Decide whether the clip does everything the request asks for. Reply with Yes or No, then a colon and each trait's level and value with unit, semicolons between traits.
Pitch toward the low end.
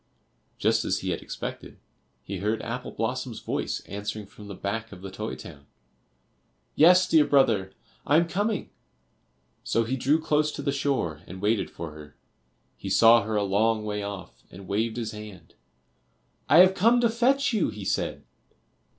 Yes: low, 110 Hz